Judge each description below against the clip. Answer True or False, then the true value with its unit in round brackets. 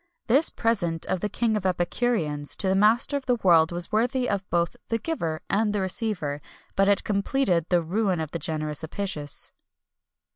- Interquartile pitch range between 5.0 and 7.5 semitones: True (5.3 semitones)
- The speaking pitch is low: False (195 Hz)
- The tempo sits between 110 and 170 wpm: False (185 wpm)